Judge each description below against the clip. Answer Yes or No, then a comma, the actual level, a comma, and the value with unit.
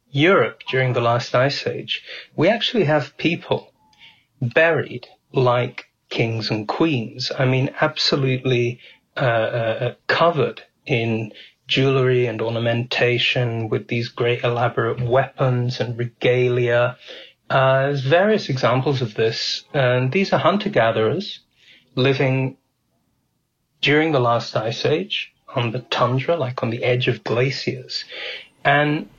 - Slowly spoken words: Yes, slow, 120 wpm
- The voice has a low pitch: Yes, low, 125 Hz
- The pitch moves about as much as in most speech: No, narrow, 2.3 semitones